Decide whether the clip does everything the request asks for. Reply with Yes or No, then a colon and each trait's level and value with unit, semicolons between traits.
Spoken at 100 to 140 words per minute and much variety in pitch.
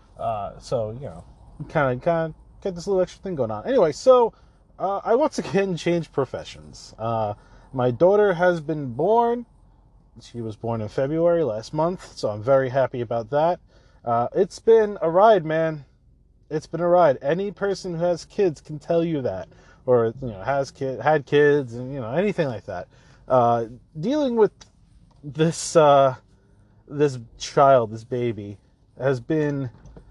No: average, 170 wpm; wide, 6.2 semitones